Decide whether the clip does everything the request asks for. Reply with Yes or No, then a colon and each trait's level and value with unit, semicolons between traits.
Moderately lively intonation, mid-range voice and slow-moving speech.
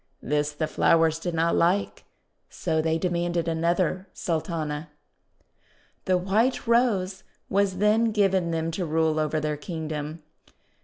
Yes: average, 3.0 semitones; medium, 170 Hz; slow, 125 wpm